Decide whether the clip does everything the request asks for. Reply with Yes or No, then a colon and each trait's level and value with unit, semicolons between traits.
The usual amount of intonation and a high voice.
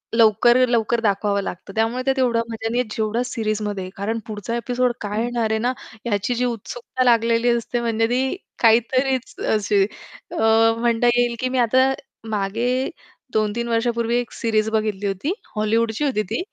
No: narrow, 2.1 semitones; high, 230 Hz